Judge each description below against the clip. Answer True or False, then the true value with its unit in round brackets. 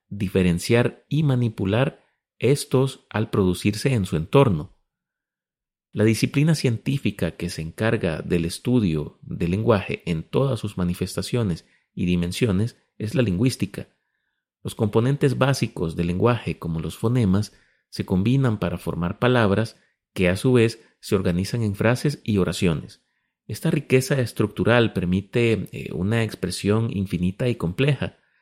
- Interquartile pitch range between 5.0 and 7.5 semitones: True (5.3 semitones)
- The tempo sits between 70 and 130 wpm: True (125 wpm)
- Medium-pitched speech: False (110 Hz)